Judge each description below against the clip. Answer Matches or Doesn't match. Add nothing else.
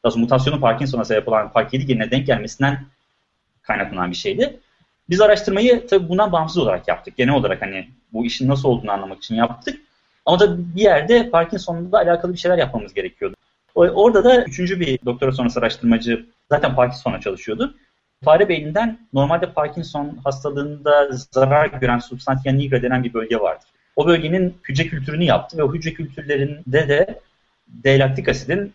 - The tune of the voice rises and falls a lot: Matches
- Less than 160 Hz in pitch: Matches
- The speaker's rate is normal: Doesn't match